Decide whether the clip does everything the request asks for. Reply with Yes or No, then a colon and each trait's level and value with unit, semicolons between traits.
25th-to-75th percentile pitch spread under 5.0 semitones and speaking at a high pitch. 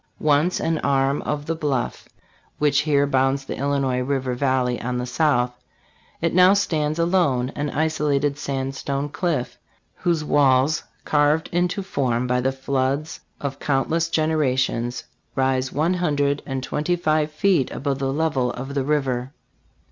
No: average, 2.7 semitones; medium, 140 Hz